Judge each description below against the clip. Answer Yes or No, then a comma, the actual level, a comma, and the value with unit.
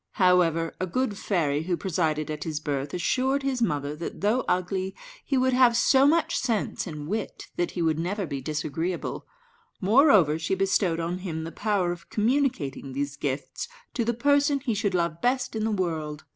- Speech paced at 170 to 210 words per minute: Yes, average, 185 wpm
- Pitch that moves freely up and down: Yes, wide, 6.7 semitones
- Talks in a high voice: No, medium, 180 Hz